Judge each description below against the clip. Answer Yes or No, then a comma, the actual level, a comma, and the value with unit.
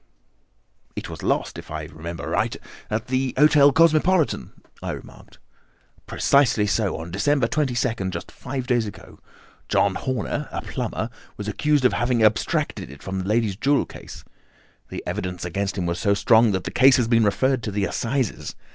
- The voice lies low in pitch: Yes, low, 115 Hz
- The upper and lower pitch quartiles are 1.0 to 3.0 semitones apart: No, average, 5.2 semitones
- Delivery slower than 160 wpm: No, average, 170 wpm